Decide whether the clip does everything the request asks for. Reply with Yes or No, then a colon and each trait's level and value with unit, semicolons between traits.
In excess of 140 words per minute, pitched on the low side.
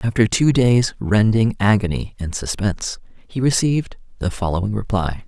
No: slow, 135 wpm; low, 110 Hz